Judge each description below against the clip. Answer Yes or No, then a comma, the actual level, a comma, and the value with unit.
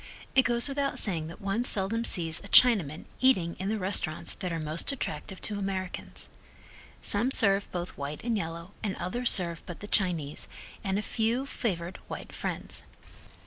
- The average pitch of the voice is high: Yes, high, 195 Hz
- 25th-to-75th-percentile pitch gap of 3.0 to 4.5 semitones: No, average, 5.1 semitones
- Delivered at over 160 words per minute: Yes, average, 170 wpm